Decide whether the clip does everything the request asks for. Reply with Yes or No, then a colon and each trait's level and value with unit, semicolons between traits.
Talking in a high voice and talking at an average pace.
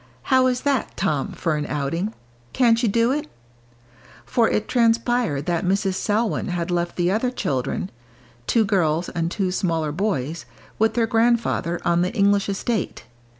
Yes: high, 195 Hz; average, 155 wpm